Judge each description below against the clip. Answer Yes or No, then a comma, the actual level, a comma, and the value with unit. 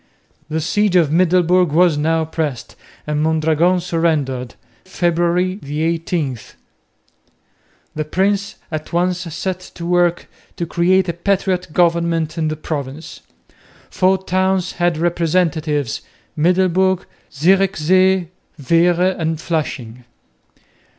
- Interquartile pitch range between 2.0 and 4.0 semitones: Yes, average, 2.8 semitones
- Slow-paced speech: Yes, slow, 105 wpm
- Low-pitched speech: No, medium, 170 Hz